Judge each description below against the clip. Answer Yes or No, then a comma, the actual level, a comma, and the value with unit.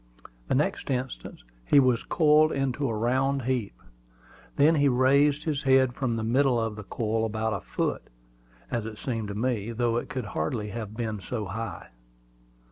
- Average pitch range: Yes, average, 3.5 semitones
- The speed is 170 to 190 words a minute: Yes, average, 175 wpm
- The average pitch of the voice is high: No, low, 120 Hz